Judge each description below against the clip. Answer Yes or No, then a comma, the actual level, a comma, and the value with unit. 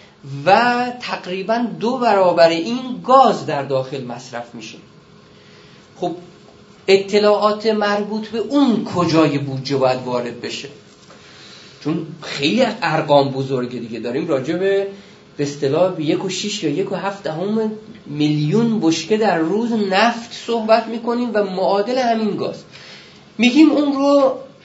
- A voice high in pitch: Yes, high, 195 Hz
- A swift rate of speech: No, average, 125 wpm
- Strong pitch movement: Yes, wide, 6.9 semitones